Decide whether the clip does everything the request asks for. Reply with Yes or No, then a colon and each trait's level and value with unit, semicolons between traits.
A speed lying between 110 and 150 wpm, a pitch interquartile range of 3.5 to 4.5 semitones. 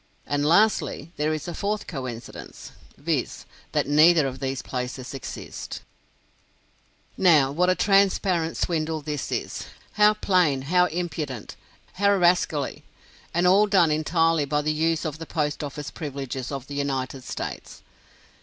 Yes: average, 140 wpm; average, 4.2 semitones